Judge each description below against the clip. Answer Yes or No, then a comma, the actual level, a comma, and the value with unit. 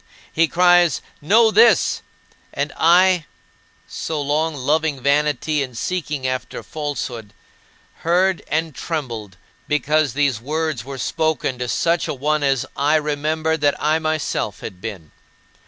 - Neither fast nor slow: No, slow, 130 wpm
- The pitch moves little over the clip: No, average, 3.2 semitones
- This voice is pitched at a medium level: Yes, medium, 150 Hz